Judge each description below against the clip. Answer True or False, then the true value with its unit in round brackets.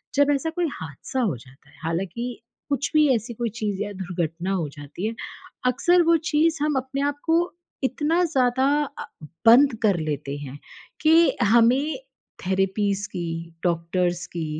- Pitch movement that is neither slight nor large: False (8.8 semitones)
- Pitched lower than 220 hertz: False (225 Hz)